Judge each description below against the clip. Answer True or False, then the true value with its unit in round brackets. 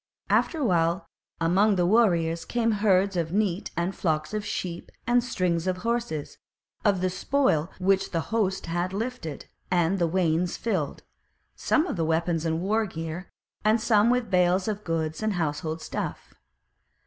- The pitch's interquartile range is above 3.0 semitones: True (4.4 semitones)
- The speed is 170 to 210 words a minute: False (160 wpm)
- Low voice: False (185 Hz)